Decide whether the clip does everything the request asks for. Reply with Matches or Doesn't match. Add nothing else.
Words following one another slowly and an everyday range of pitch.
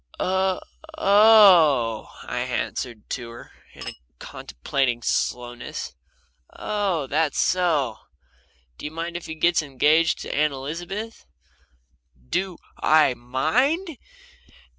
Doesn't match